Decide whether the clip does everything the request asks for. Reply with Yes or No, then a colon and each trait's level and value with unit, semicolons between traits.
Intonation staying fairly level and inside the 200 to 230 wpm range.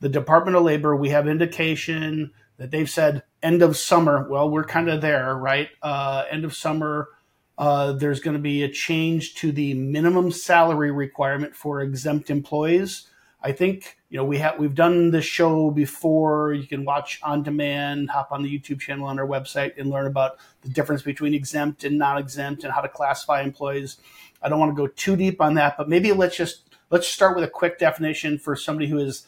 Yes: narrow, 2.2 semitones; fast, 205 wpm